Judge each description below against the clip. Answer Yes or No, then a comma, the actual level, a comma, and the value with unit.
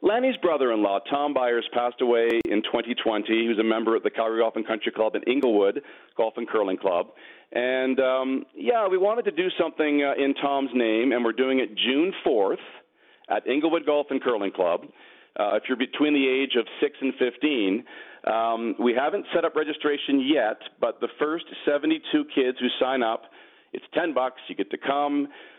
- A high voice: No, low, 135 Hz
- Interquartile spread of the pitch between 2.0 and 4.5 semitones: No, wide, 5.6 semitones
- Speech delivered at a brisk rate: No, average, 195 wpm